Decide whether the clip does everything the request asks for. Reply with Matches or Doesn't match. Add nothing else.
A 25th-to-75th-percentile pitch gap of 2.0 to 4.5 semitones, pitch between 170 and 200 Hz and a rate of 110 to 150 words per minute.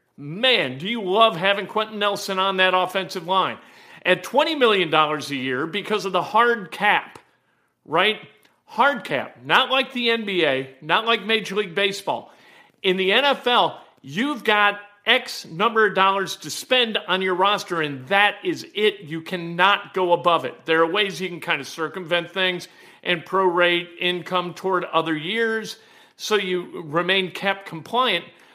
Doesn't match